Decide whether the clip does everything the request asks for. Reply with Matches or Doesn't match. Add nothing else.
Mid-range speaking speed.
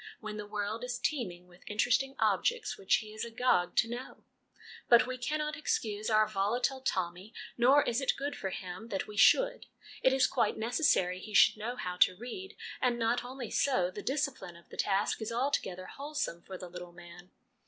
Matches